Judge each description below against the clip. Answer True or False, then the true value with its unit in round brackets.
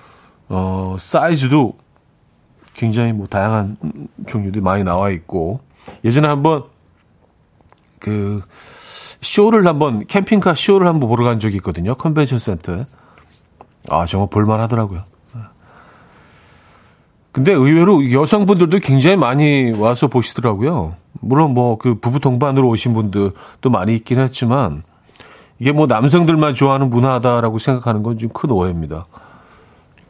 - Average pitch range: False (5.9 semitones)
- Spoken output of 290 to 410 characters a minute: False (275 characters per minute)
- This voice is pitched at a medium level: False (120 Hz)